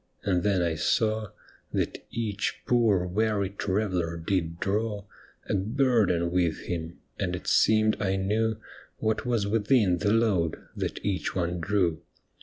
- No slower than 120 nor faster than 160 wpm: Yes, average, 140 wpm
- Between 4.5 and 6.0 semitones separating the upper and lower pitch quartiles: No, average, 3.5 semitones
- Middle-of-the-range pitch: No, low, 100 Hz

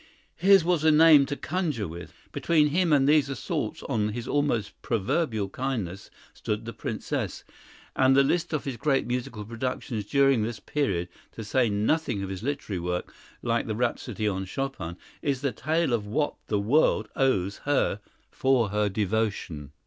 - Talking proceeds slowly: No, average, 165 wpm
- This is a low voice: Yes, low, 120 Hz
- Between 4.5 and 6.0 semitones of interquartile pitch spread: Yes, wide, 5.6 semitones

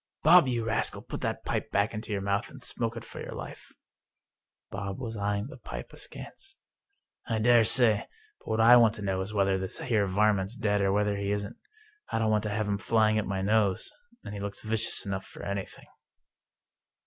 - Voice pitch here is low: Yes, low, 105 Hz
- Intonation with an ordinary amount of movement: No, narrow, 2.1 semitones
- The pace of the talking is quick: Yes, fast, 220 wpm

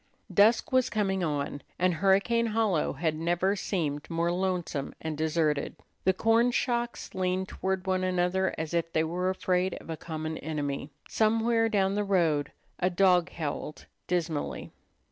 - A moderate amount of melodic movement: Yes, average, 3.6 semitones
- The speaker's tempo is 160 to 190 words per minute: No, average, 150 wpm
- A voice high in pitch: No, medium, 180 Hz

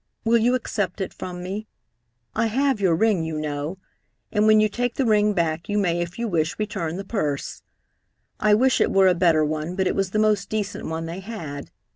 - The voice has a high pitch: Yes, high, 195 Hz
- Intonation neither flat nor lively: Yes, average, 4.3 semitones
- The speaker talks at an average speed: No, fast, 215 wpm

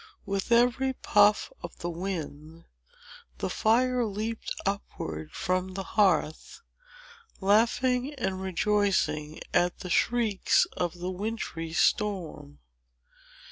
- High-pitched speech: Yes, high, 195 Hz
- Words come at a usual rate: No, slow, 100 wpm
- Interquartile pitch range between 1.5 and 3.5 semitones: No, average, 4.2 semitones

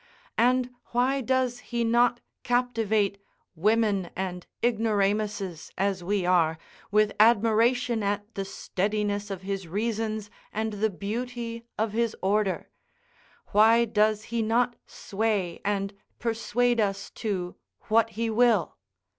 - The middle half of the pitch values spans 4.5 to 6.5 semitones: No, average, 2.7 semitones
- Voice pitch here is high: Yes, high, 215 Hz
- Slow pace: Yes, slow, 120 wpm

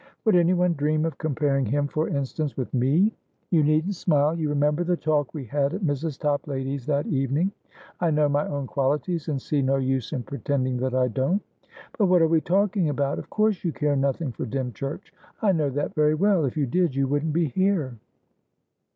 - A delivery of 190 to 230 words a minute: Yes, average, 195 wpm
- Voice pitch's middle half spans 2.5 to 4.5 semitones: Yes, average, 3.4 semitones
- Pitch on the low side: No, medium, 150 Hz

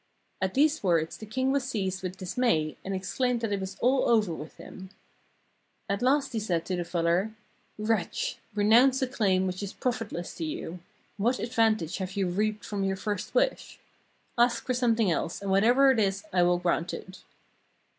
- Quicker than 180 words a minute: Yes, average, 190 wpm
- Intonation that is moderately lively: Yes, average, 4.5 semitones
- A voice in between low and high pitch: No, high, 205 Hz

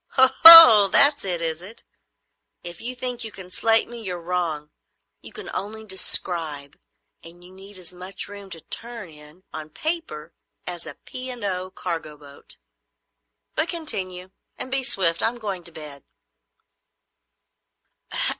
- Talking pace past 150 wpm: No, average, 145 wpm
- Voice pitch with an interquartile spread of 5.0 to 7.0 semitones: Yes, wide, 5.6 semitones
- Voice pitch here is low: No, medium, 185 Hz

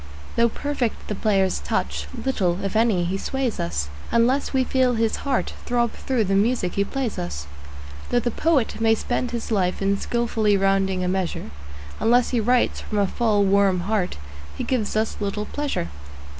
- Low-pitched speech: No, high, 215 Hz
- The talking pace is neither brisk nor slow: Yes, average, 175 wpm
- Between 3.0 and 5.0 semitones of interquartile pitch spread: Yes, average, 3.9 semitones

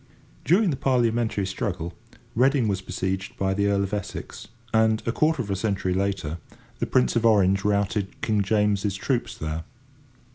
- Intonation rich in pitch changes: No, average, 3.2 semitones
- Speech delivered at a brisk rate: No, average, 160 wpm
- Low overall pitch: Yes, low, 100 Hz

